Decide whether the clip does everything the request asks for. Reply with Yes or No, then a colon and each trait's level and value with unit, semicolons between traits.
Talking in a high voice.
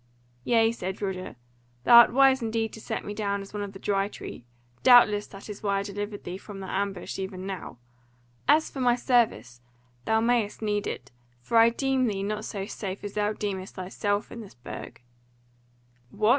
Yes: high, 205 Hz